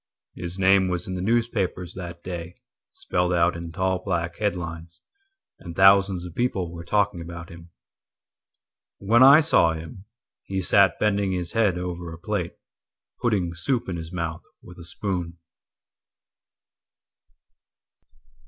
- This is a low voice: Yes, very low, 90 Hz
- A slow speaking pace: Yes, slow, 120 wpm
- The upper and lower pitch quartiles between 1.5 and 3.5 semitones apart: Yes, average, 2.8 semitones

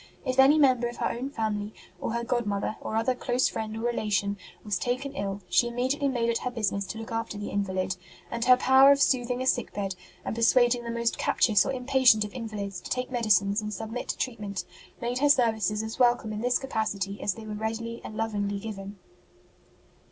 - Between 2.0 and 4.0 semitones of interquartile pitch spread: Yes, average, 3.1 semitones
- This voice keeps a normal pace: No, fast, 210 wpm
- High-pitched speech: Yes, high, 230 Hz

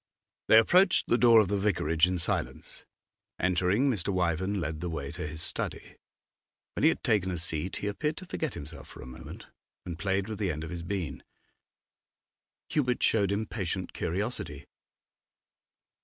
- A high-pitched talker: No, very low, 95 Hz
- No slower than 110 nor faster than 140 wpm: No, average, 165 wpm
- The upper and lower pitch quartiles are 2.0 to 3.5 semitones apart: No, average, 4.6 semitones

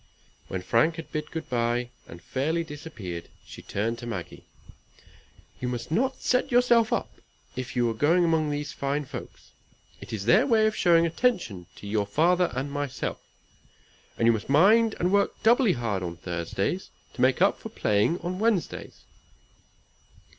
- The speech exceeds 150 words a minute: Yes, average, 160 wpm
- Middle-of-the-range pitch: Yes, medium, 145 Hz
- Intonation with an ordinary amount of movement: No, wide, 7.8 semitones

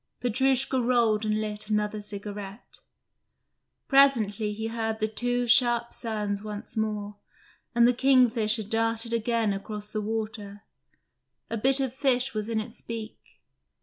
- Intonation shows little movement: Yes, narrow, 2.2 semitones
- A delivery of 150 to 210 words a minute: No, slow, 135 wpm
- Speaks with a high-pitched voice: Yes, high, 220 Hz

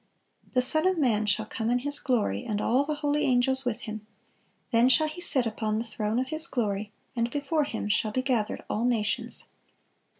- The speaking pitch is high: Yes, high, 245 Hz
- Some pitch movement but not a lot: Yes, average, 4.6 semitones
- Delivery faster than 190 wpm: Yes, fast, 205 wpm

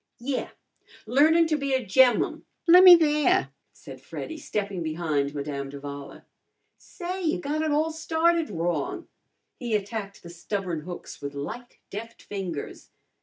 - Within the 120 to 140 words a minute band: Yes, slow, 135 wpm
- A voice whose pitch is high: Yes, high, 225 Hz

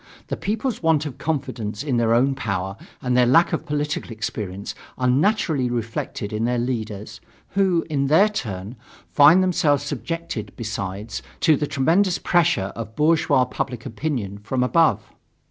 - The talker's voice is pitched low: Yes, low, 130 Hz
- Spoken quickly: No, average, 150 wpm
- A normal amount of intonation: No, wide, 6.2 semitones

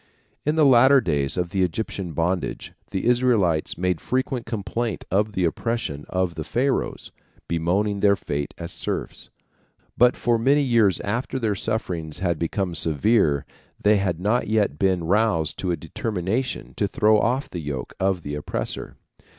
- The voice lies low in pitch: Yes, low, 100 Hz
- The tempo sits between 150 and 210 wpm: Yes, average, 160 wpm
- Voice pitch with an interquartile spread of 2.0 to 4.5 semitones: No, average, 5.3 semitones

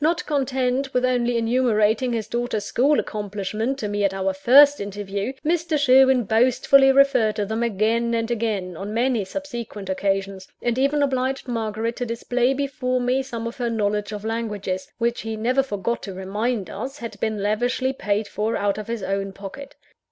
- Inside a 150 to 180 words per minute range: Yes, average, 175 wpm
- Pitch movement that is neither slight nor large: Yes, average, 3.8 semitones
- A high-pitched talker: Yes, high, 230 Hz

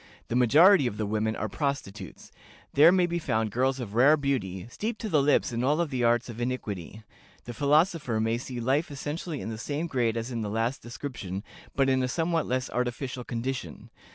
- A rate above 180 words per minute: Yes, average, 200 wpm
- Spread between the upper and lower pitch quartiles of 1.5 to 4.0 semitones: No, average, 4.4 semitones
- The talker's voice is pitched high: No, low, 125 Hz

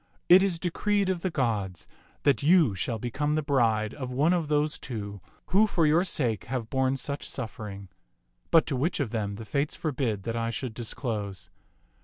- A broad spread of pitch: Yes, wide, 5.9 semitones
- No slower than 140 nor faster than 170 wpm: No, average, 185 wpm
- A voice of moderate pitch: No, low, 130 Hz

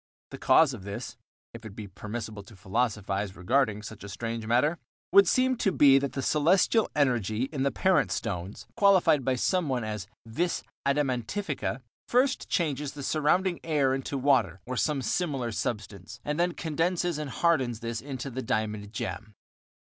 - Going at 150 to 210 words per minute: Yes, average, 165 wpm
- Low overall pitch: Yes, low, 130 Hz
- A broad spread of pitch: Yes, wide, 6.1 semitones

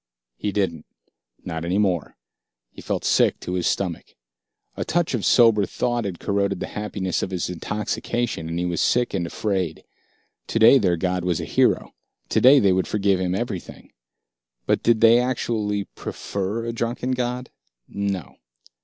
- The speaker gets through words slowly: No, average, 160 wpm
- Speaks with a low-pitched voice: Yes, low, 100 Hz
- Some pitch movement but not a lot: Yes, average, 4.3 semitones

